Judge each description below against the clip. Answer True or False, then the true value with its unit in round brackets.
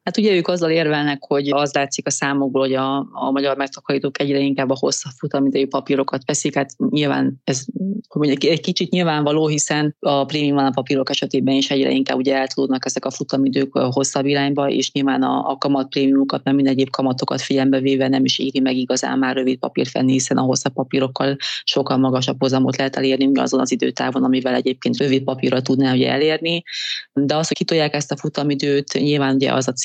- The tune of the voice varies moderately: False (1.3 semitones)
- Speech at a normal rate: False (195 wpm)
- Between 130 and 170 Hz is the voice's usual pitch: True (135 Hz)